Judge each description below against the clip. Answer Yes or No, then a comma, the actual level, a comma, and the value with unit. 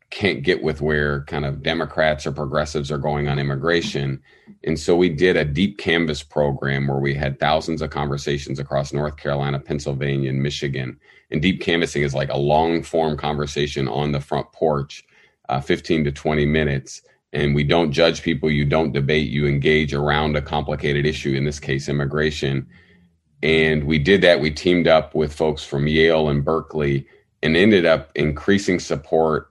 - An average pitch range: No, narrow, 1.8 semitones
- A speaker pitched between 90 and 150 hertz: No, very low, 75 Hz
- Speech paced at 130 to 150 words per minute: No, average, 175 wpm